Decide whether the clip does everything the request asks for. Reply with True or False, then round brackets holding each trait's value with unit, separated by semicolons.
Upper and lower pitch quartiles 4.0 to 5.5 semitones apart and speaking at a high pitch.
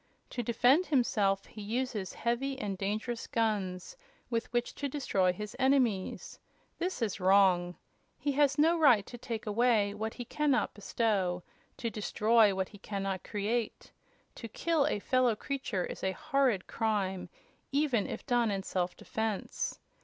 True (4.4 semitones; 220 Hz)